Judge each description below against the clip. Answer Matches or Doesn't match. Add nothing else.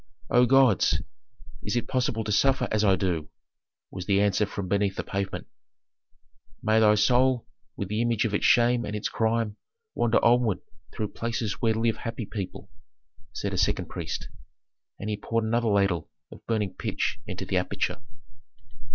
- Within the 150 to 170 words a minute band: Matches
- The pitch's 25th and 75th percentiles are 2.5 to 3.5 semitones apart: Matches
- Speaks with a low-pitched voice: Matches